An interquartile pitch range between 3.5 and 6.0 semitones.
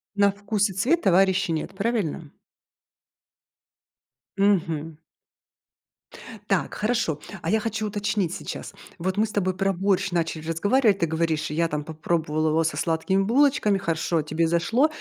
Yes: average, 4.1 semitones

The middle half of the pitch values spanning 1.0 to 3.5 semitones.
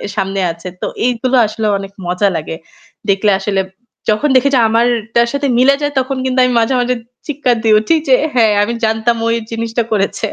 Yes: average, 3.0 semitones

